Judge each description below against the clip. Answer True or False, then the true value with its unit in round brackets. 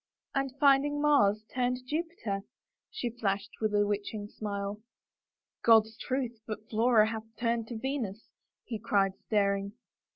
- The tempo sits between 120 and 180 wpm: True (135 wpm)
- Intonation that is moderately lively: True (3.6 semitones)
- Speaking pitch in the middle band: False (225 Hz)